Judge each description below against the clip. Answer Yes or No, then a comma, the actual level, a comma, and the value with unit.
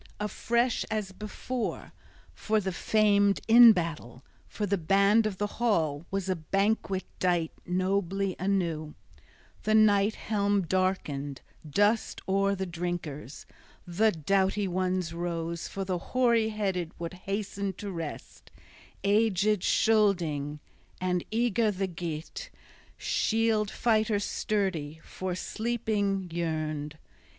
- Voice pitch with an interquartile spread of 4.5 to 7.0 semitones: No, average, 3.6 semitones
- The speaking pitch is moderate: No, high, 195 Hz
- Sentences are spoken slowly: Yes, slow, 115 wpm